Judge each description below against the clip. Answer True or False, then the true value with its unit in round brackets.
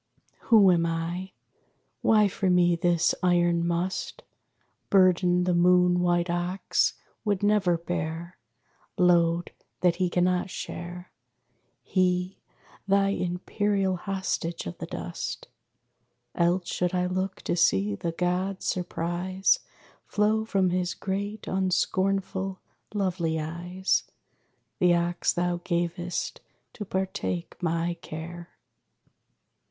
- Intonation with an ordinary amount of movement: False (1.6 semitones)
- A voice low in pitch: False (180 Hz)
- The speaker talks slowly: True (105 wpm)